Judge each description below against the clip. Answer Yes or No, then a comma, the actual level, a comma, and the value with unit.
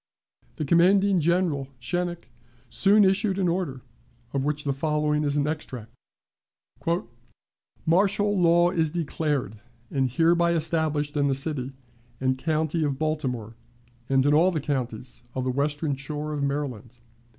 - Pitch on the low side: No, medium, 150 Hz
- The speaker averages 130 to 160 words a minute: Yes, average, 140 wpm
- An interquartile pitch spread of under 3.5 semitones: No, average, 3.9 semitones